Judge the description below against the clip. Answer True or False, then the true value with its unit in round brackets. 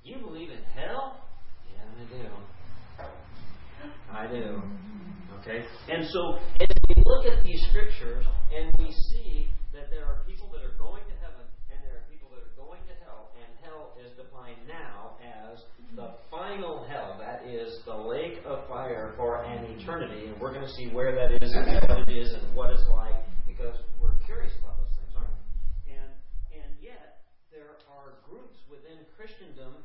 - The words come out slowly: False (180 wpm)